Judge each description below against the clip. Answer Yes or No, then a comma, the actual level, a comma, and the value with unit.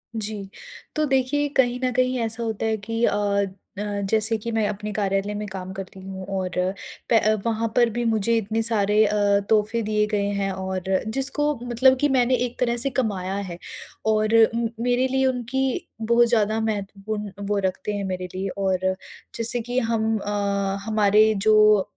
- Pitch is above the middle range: Yes, high, 220 Hz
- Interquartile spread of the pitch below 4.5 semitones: Yes, average, 2.8 semitones